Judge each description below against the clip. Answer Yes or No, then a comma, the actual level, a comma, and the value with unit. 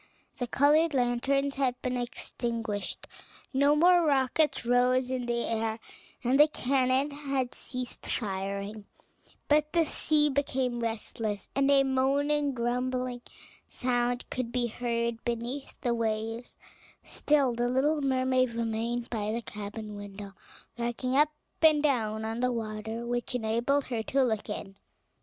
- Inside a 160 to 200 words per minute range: No, slow, 135 wpm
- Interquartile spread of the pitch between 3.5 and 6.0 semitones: No, average, 3.1 semitones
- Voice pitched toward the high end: Yes, high, 245 Hz